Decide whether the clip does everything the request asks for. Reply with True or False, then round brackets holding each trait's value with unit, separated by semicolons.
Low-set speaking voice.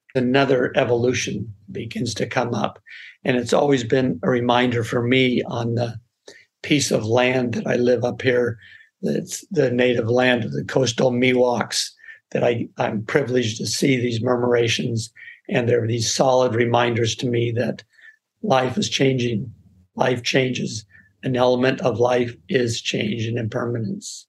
True (125 Hz)